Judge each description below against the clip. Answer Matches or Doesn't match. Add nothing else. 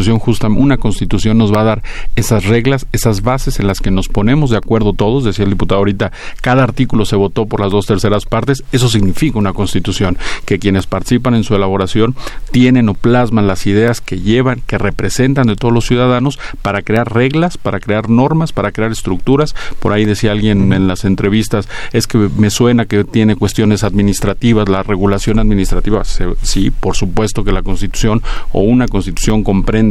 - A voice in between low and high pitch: Doesn't match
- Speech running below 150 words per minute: Doesn't match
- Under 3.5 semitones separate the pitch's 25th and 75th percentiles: Matches